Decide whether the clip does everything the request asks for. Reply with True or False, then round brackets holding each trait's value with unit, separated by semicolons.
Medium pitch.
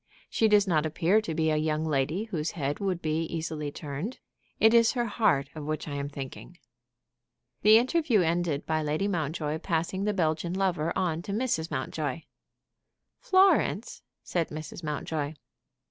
True (160 Hz)